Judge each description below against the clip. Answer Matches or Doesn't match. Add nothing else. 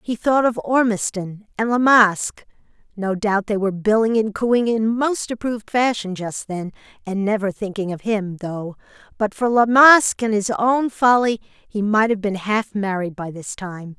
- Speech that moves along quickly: Doesn't match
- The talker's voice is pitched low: Doesn't match